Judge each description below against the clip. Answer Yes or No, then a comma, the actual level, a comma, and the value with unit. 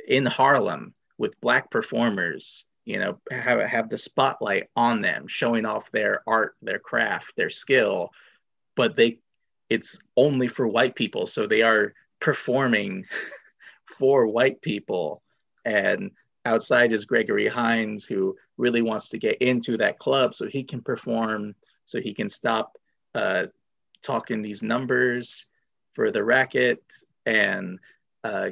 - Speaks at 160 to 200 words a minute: No, slow, 135 wpm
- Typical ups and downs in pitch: No, narrow, 2.2 semitones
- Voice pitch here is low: Yes, low, 120 Hz